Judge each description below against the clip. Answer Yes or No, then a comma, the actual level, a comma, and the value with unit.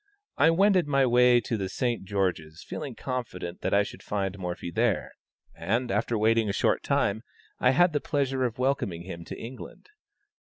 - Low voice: Yes, low, 115 Hz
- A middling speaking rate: Yes, average, 180 wpm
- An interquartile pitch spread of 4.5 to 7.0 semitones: Yes, average, 5.0 semitones